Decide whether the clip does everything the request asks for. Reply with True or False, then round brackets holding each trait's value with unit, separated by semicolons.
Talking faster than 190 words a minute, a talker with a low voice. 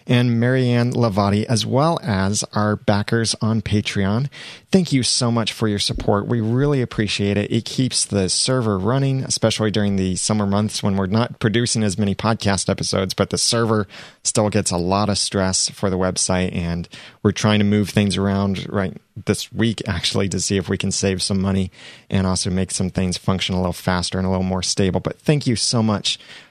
True (200 wpm; 105 Hz)